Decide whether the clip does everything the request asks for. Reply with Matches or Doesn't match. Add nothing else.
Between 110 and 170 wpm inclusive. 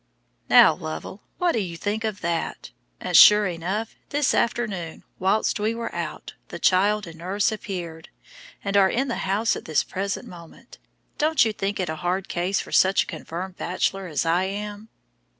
Doesn't match